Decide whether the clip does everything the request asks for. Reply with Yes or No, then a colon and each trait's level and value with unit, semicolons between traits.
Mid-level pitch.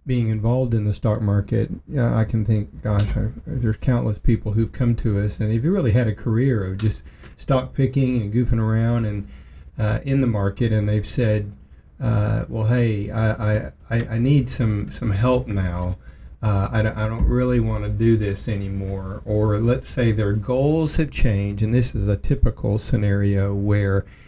No: low, 110 Hz